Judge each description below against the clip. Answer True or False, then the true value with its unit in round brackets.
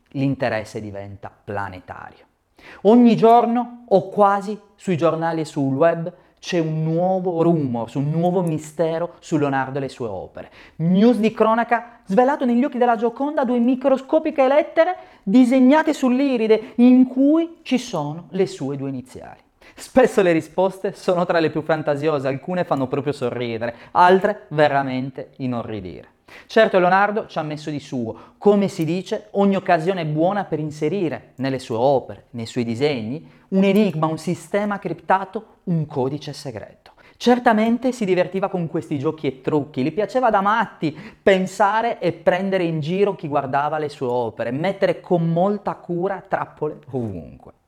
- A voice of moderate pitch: True (175 Hz)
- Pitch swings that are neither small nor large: False (6.5 semitones)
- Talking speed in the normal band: True (150 wpm)